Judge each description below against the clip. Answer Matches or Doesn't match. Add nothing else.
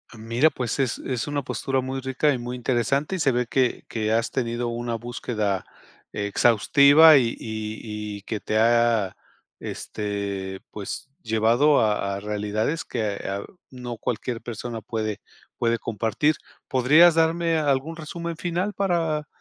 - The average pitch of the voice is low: Matches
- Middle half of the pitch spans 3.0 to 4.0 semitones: Doesn't match